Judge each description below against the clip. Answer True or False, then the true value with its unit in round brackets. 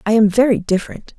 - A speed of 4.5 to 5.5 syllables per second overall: False (6.6 syllables/s)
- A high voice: True (215 Hz)